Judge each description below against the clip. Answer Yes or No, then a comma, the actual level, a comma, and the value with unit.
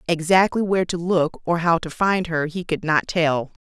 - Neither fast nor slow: No, fast, 215 wpm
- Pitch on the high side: No, medium, 170 Hz